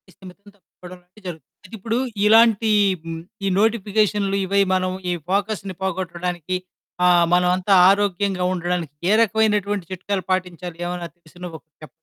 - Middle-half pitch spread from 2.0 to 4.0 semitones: Yes, narrow, 2.4 semitones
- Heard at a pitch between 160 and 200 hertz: Yes, medium, 185 Hz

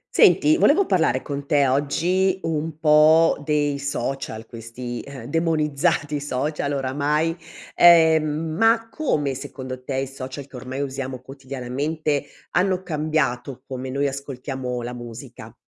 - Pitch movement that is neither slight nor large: Yes, average, 3.3 semitones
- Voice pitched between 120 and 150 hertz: Yes, medium, 140 Hz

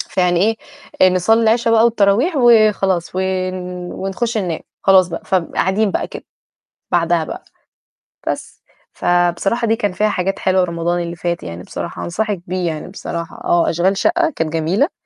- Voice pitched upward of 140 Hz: Yes, medium, 185 Hz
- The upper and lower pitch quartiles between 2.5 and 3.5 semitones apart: No, average, 4.0 semitones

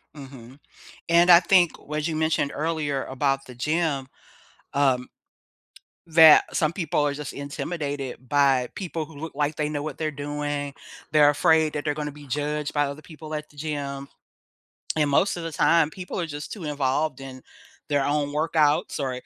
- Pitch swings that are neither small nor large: No, narrow, 1.9 semitones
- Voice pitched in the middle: Yes, medium, 150 Hz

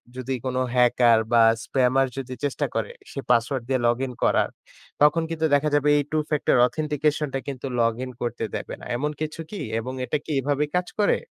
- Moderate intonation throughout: Yes, average, 3.2 semitones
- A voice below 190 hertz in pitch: Yes, low, 135 Hz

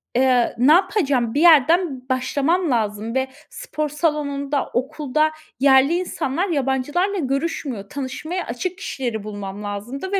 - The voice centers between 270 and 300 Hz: Yes, very high, 275 Hz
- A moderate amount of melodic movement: Yes, average, 4.5 semitones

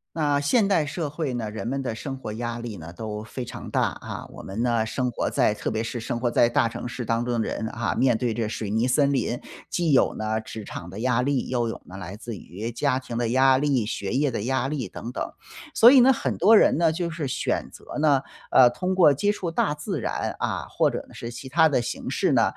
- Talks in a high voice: No, low, 125 Hz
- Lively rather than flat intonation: No, average, 4.3 semitones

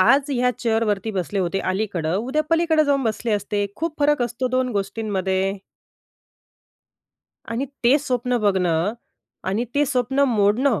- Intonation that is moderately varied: Yes, average, 5.0 semitones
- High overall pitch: Yes, high, 225 Hz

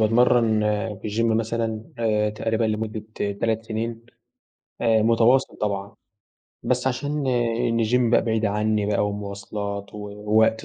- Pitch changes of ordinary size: No, narrow, 1.6 semitones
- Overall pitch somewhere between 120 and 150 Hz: No, low, 110 Hz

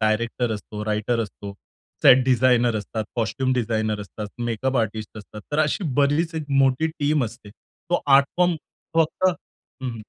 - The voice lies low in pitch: Yes, low, 120 Hz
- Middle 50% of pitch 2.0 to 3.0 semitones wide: No, average, 4.4 semitones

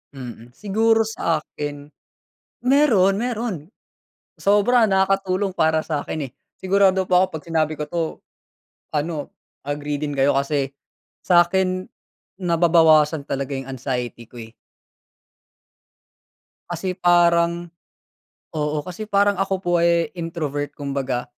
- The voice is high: No, medium, 170 Hz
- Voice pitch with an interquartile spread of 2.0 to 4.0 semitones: No, average, 4.7 semitones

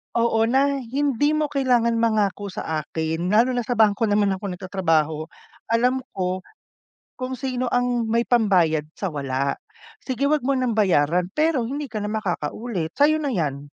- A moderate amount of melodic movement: No, wide, 6.1 semitones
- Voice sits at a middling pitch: No, high, 225 Hz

